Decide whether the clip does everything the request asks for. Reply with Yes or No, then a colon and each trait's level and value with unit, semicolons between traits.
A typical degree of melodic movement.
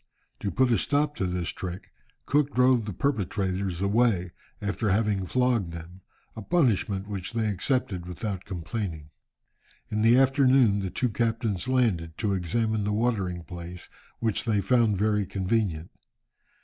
Yes: average, 4.2 semitones